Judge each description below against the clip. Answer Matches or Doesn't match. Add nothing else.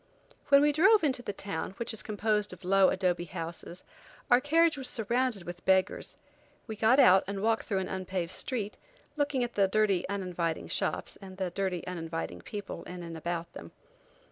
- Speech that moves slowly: Doesn't match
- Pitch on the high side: Matches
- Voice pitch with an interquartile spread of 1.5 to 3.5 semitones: Doesn't match